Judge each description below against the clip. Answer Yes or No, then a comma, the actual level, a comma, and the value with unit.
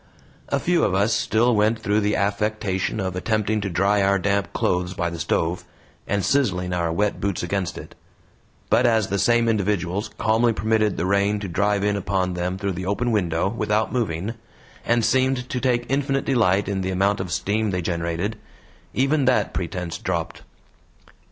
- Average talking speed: Yes, average, 175 wpm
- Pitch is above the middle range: No, low, 100 Hz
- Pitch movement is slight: No, average, 3.3 semitones